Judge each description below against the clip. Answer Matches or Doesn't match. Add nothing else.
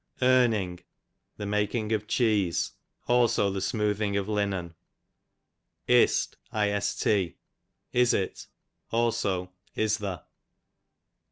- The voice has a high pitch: Doesn't match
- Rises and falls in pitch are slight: Matches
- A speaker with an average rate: Doesn't match